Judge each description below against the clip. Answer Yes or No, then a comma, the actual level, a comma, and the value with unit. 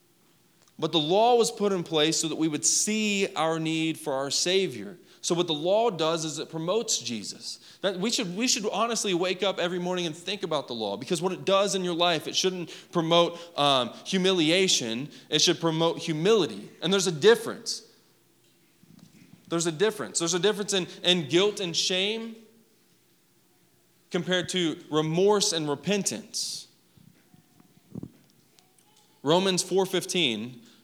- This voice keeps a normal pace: Yes, average, 155 wpm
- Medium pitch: Yes, medium, 175 Hz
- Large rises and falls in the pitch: No, average, 3.3 semitones